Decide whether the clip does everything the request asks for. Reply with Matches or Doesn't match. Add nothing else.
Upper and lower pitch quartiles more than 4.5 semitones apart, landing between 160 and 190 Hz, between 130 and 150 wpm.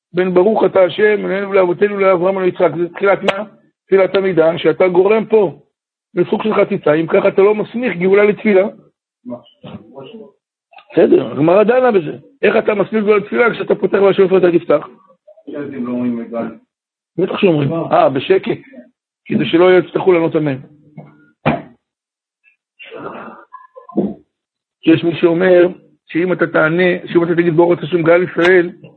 Doesn't match